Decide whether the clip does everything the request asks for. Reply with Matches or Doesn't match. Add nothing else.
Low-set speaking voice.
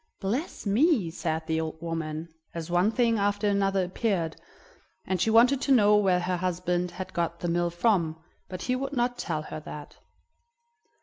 Doesn't match